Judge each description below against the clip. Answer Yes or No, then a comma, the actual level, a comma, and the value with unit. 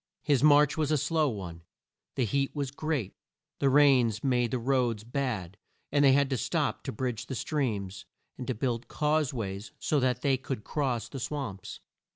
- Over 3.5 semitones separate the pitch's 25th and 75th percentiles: Yes, average, 4.0 semitones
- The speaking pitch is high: No, low, 130 Hz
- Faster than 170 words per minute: Yes, average, 185 wpm